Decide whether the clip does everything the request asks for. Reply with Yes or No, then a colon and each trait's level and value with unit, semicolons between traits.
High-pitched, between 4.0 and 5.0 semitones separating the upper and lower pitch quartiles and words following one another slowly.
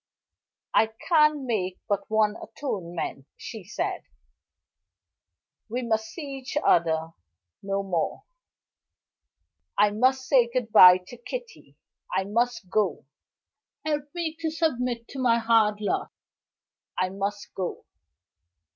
Yes: high, 225 Hz; average, 4.7 semitones; slow, 115 wpm